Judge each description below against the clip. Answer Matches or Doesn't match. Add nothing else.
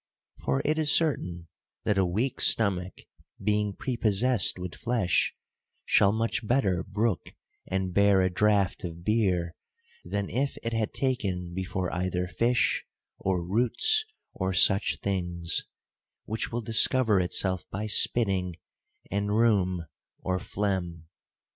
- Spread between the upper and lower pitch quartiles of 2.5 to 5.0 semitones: Matches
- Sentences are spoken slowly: Matches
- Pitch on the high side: Doesn't match